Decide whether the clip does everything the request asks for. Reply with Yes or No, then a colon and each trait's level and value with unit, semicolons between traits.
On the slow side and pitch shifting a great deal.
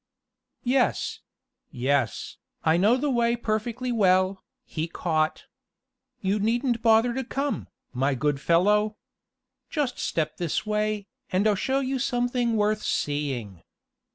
Yes: slow, 125 wpm; wide, 6.7 semitones